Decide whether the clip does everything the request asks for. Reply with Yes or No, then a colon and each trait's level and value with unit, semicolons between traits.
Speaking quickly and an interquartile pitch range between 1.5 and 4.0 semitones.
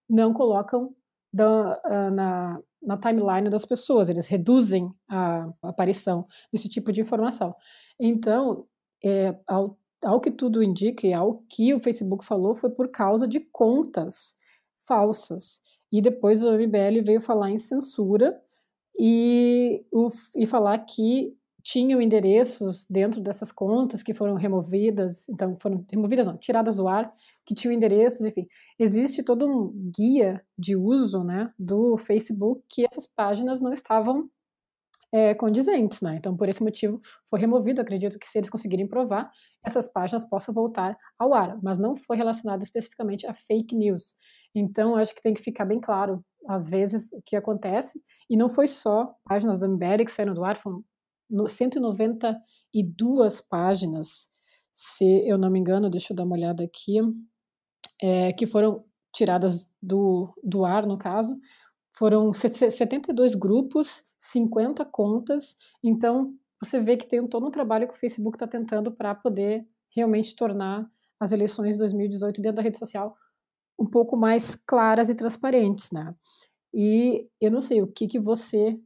No: average, 155 wpm; average, 3.0 semitones